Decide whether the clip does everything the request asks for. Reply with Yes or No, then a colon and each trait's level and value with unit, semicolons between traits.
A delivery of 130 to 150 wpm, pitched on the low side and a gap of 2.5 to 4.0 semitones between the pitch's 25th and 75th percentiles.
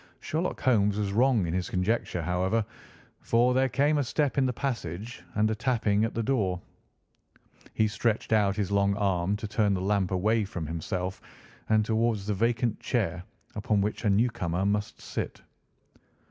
No: average, 170 wpm; low, 105 Hz; average, 3.1 semitones